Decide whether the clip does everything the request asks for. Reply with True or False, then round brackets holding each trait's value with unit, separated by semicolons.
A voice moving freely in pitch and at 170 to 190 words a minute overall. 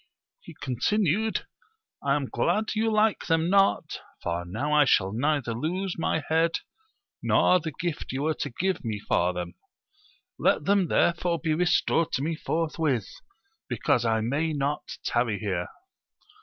False (6.6 semitones; 155 wpm)